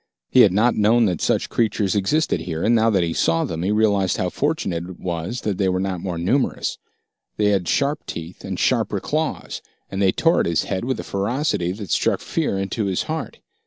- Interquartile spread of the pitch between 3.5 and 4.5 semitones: Yes, average, 4.2 semitones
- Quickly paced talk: Yes, fast, 215 wpm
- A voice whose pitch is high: No, low, 100 Hz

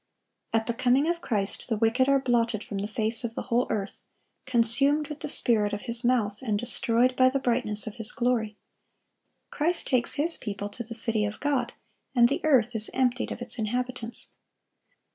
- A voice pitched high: Yes, high, 235 Hz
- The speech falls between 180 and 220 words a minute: Yes, average, 190 wpm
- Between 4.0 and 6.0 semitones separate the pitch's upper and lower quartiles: No, average, 2.7 semitones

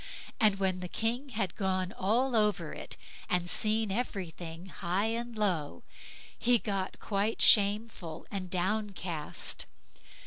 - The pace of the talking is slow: Yes, slow, 125 wpm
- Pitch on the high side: Yes, high, 195 Hz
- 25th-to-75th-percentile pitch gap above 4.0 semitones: No, average, 3.4 semitones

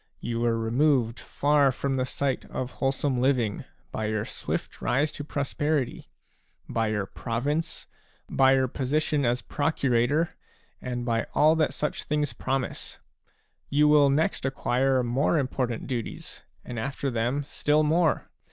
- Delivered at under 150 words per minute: Yes, average, 140 wpm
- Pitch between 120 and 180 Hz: Yes, low, 135 Hz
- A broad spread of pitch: No, average, 3.4 semitones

